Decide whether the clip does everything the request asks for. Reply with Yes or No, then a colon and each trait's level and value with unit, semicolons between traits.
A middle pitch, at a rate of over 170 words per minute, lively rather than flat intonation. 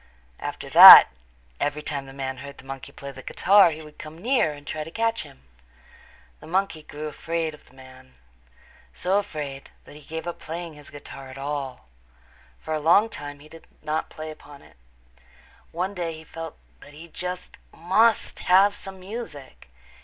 No: medium, 155 Hz; average, 185 wpm; average, 3.6 semitones